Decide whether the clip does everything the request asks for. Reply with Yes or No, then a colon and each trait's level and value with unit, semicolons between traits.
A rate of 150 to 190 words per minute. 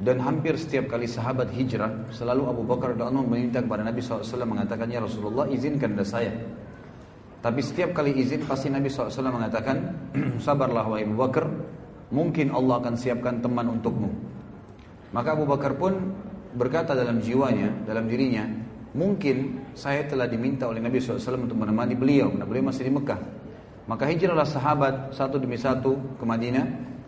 Yes: average, 155 wpm